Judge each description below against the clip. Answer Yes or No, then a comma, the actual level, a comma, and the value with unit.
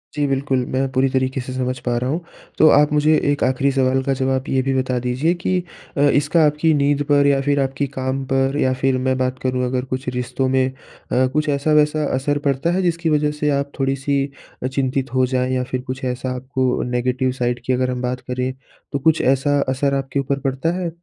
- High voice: No, low, 135 Hz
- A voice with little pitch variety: Yes, narrow, 1.9 semitones